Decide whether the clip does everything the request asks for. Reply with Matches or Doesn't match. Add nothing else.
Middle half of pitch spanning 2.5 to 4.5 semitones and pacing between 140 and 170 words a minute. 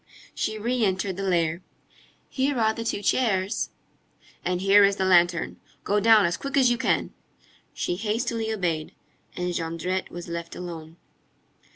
Matches